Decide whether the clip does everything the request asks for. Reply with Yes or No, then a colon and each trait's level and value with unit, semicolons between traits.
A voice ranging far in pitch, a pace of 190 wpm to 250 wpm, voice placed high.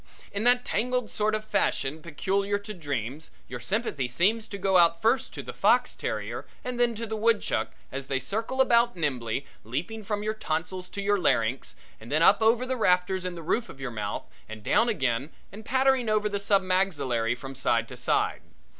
Yes: wide, 8.2 semitones; average, 200 wpm; high, 195 Hz